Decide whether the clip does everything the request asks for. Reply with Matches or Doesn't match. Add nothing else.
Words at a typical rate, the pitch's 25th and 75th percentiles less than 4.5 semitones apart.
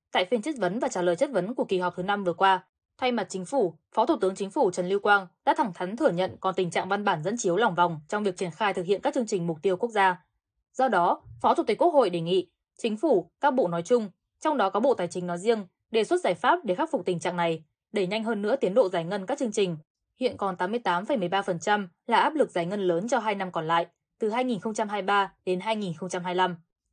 Doesn't match